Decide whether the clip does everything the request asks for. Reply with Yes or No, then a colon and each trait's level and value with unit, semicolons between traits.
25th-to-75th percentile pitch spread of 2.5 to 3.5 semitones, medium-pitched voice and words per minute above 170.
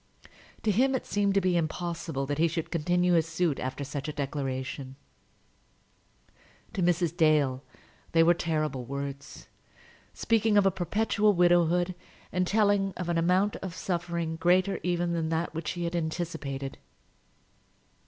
No: average, 2.9 semitones; medium, 170 Hz; average, 145 wpm